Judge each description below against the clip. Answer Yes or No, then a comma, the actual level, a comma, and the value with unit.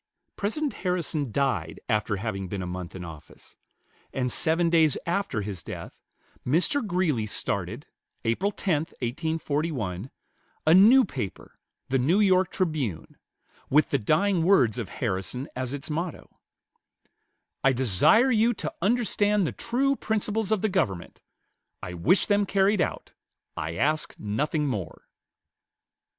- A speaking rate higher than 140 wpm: No, slow, 135 wpm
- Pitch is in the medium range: Yes, medium, 150 Hz